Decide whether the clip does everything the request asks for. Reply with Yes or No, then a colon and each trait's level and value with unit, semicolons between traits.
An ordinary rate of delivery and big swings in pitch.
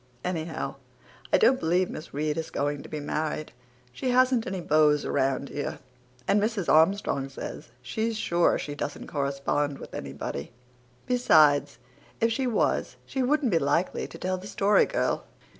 Yes: average, 160 wpm; wide, 6.4 semitones